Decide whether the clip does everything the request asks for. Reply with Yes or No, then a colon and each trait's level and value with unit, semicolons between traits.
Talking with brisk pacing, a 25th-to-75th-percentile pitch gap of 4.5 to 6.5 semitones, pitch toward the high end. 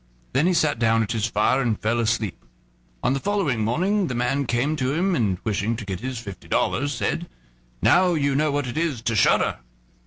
No: fast, 210 wpm; average, 4.8 semitones; low, 125 Hz